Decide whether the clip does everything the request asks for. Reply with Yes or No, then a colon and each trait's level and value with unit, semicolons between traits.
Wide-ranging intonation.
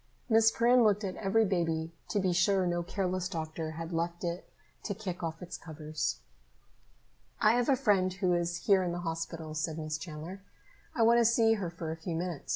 No: average, 3.6 semitones